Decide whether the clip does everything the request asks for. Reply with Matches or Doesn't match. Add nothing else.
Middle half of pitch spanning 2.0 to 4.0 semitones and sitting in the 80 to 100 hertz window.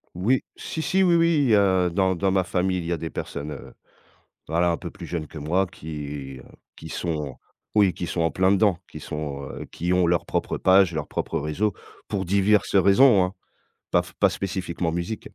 Matches